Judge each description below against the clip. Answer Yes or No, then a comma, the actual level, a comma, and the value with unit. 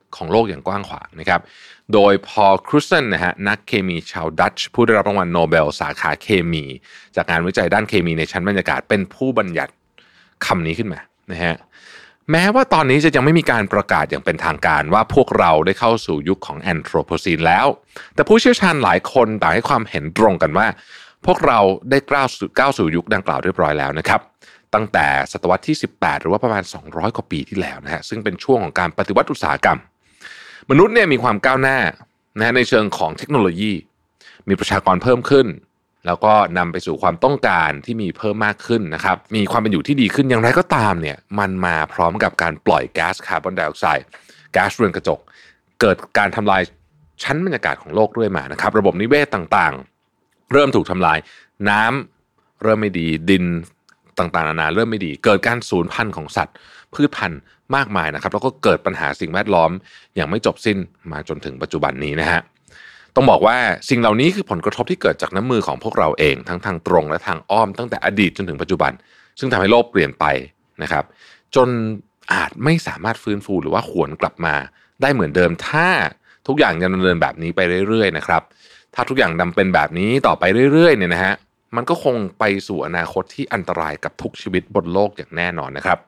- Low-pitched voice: Yes, low, 100 Hz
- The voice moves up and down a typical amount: No, wide, 5.9 semitones